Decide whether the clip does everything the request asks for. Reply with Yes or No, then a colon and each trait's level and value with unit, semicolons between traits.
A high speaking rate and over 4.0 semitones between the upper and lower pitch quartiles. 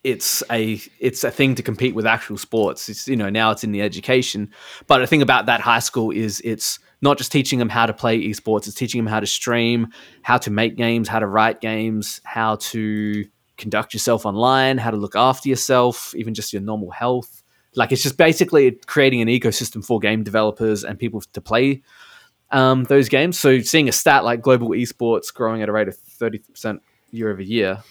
No: fast, 210 wpm; average, 2.8 semitones